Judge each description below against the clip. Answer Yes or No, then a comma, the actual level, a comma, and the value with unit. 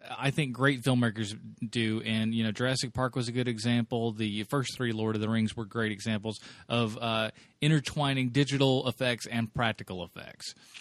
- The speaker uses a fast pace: No, average, 180 wpm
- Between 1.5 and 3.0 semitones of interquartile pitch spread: Yes, average, 2.7 semitones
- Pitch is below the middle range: Yes, low, 120 Hz